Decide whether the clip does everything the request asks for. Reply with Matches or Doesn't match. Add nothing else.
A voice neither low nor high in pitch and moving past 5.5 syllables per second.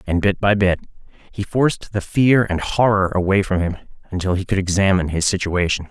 Doesn't match